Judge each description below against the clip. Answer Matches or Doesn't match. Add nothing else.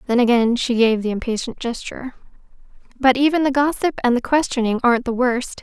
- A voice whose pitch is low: Doesn't match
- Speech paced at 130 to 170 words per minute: Doesn't match